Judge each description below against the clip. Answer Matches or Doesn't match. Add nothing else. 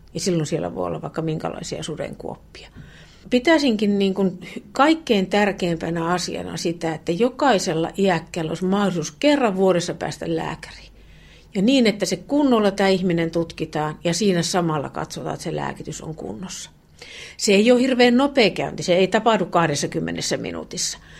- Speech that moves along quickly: Doesn't match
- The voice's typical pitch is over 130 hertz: Matches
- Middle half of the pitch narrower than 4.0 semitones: Doesn't match